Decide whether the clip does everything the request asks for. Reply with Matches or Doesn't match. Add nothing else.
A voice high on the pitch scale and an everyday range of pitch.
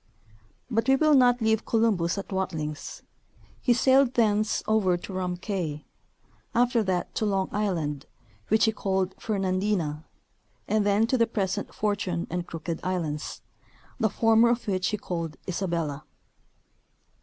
Matches